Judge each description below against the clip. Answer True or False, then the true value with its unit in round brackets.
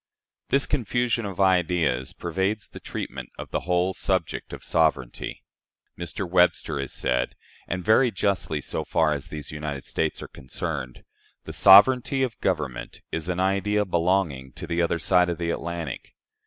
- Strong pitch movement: False (4.1 semitones)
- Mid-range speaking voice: False (85 Hz)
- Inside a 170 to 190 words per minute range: False (155 wpm)